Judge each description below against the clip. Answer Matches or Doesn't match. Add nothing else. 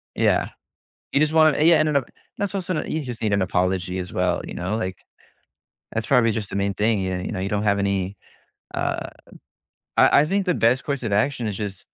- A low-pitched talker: Matches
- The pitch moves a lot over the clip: Matches